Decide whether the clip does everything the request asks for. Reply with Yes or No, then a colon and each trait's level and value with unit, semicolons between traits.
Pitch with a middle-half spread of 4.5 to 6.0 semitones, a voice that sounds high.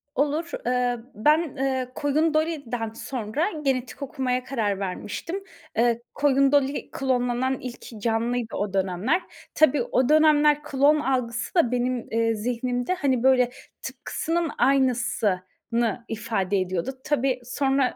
No: average, 3.5 semitones; very high, 255 Hz